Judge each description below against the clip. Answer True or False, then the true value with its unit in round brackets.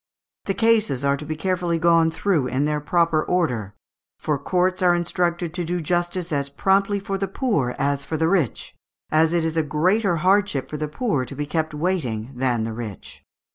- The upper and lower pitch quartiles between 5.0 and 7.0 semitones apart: False (4.3 semitones)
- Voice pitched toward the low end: False (160 Hz)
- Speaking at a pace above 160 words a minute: True (195 wpm)